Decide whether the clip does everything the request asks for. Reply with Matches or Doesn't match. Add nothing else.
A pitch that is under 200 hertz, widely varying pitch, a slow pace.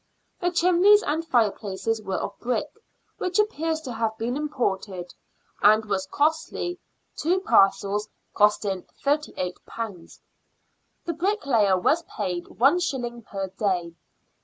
Doesn't match